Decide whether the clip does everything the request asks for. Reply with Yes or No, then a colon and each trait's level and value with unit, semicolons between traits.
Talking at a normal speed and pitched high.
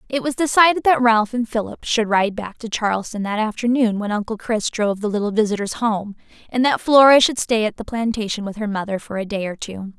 No: fast, 230 wpm; high, 220 Hz